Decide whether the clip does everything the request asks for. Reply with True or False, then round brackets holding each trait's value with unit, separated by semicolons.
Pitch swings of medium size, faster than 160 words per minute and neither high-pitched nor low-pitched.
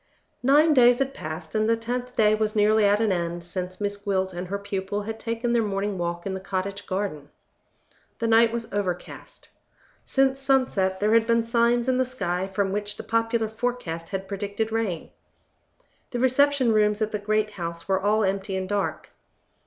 False (3.3 semitones; 185 wpm; 210 Hz)